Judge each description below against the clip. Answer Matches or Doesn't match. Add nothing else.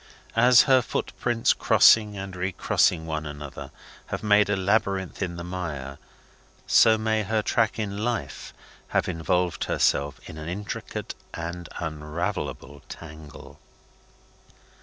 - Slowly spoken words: Matches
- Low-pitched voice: Matches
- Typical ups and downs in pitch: Matches